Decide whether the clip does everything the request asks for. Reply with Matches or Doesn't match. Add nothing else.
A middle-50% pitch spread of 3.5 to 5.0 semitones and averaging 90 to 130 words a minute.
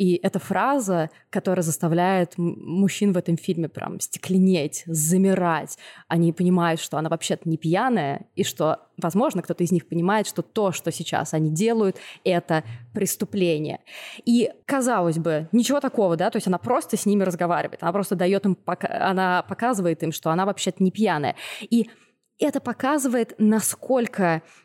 Doesn't match